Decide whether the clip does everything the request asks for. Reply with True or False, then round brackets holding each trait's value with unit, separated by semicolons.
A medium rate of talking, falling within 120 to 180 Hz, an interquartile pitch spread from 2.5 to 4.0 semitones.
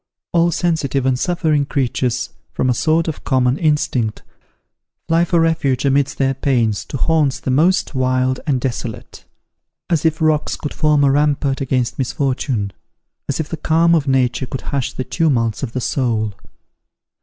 True (160 wpm; 135 Hz; 3.6 semitones)